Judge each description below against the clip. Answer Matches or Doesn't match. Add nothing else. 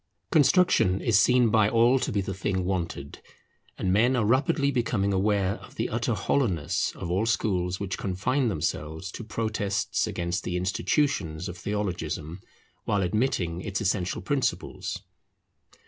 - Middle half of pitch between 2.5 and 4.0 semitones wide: Doesn't match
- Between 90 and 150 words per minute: Matches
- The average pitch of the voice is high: Doesn't match